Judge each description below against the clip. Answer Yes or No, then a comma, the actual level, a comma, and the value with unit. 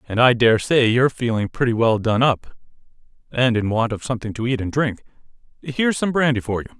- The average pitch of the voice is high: No, low, 120 Hz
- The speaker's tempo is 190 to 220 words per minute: Yes, average, 195 wpm